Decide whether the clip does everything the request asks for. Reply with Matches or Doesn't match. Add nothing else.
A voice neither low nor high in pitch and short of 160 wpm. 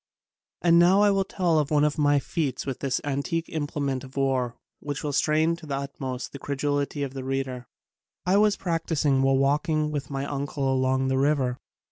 Doesn't match